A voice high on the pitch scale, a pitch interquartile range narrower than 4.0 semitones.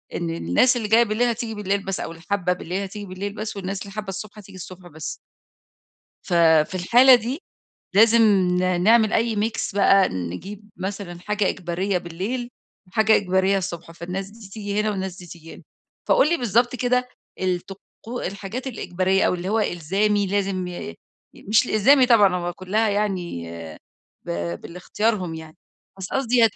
Yes: high, 200 Hz; average, 3.3 semitones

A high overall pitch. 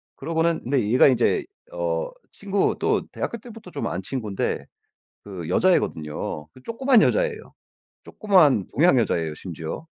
No: medium, 165 Hz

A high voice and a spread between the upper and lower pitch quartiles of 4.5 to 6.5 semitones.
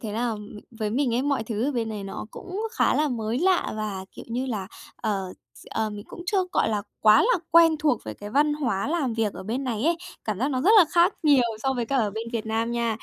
Yes: high, 235 Hz; average, 5.2 semitones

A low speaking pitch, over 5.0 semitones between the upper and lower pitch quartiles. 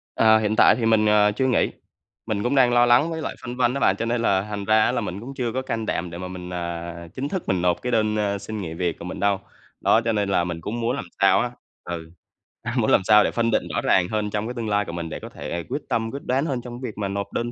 No: low, 105 Hz; average, 4.3 semitones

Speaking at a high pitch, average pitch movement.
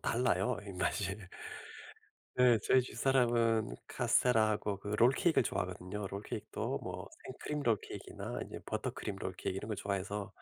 No: low, 105 Hz; average, 3.7 semitones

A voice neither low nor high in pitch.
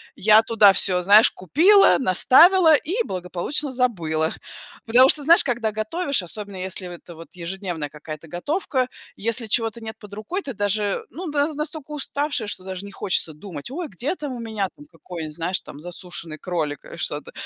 No: high, 215 Hz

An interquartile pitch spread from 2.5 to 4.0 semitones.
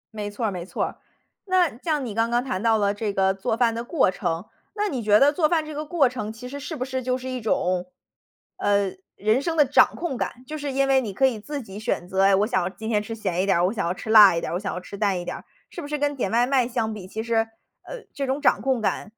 No: average, 5.2 semitones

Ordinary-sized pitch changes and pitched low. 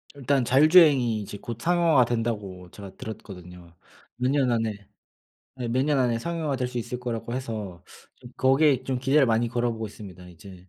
Yes: average, 4.1 semitones; low, 120 Hz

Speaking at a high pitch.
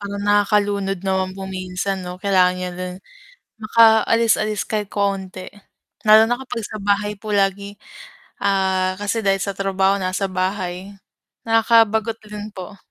Yes: high, 200 Hz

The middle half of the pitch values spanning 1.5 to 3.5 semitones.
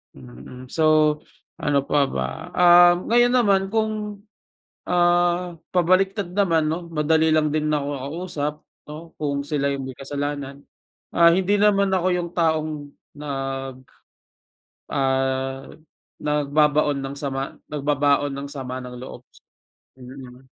No: average, 4.1 semitones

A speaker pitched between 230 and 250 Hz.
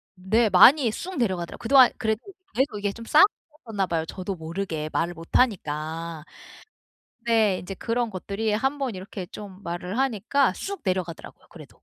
No: high, 205 Hz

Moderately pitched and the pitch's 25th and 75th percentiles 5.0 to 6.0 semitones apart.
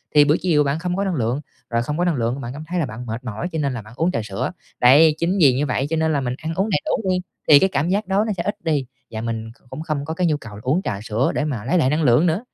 Yes: medium, 150 Hz; wide, 5.5 semitones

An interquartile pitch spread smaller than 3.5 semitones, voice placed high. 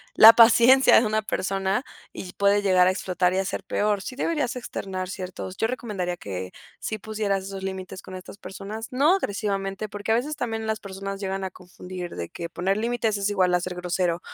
Yes: average, 2.9 semitones; high, 195 Hz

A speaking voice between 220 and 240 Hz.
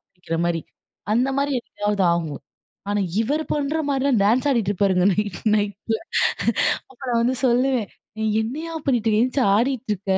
Yes: high, 225 Hz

